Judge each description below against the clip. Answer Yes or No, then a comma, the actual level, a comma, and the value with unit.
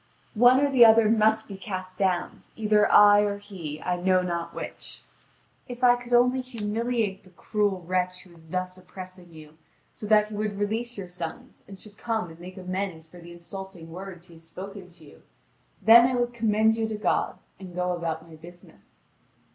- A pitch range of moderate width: Yes, average, 3.7 semitones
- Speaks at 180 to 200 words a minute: Yes, average, 195 wpm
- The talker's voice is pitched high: Yes, high, 195 Hz